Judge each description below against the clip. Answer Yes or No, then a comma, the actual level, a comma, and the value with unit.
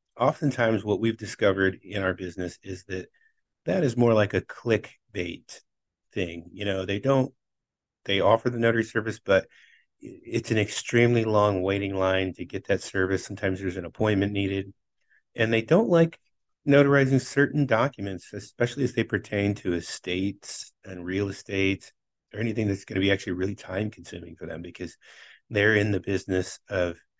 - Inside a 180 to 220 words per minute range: No, average, 165 wpm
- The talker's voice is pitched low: Yes, low, 100 Hz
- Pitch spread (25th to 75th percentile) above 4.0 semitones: No, average, 3.5 semitones